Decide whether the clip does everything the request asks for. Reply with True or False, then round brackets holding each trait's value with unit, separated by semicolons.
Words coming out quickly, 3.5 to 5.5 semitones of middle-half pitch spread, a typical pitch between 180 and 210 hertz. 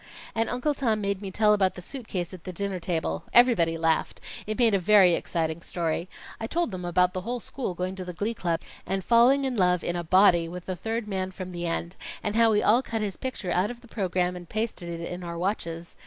True (245 wpm; 4.1 semitones; 185 Hz)